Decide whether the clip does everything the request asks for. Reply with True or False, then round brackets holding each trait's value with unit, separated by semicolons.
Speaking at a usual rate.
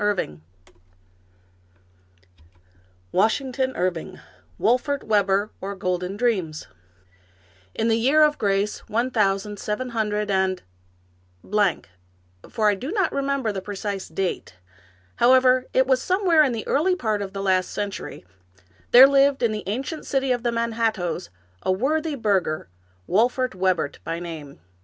True (145 wpm)